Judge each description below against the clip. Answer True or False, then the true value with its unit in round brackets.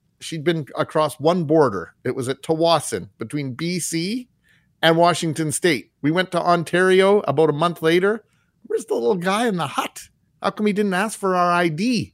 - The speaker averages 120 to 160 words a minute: False (185 wpm)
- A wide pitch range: False (2.8 semitones)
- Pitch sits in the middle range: True (170 Hz)